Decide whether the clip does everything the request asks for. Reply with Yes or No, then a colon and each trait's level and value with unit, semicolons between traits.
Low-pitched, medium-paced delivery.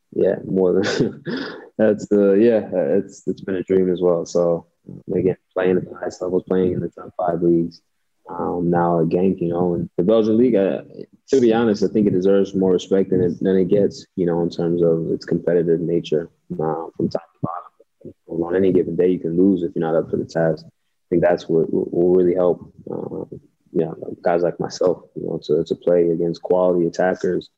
No: very low, 90 Hz; fast, 220 wpm